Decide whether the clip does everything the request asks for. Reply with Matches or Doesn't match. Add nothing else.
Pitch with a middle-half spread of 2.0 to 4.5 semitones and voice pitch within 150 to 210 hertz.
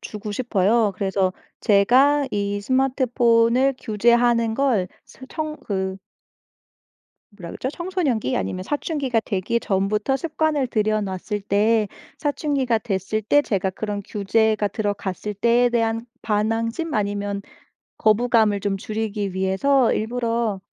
Doesn't match